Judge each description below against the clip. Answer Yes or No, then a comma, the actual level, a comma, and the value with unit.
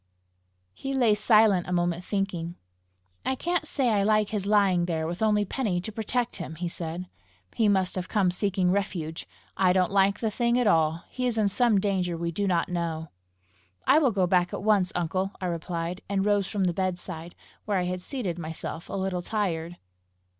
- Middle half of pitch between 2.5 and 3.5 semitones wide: Yes, average, 3.2 semitones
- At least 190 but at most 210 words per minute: Yes, average, 195 wpm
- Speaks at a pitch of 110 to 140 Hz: No, high, 190 Hz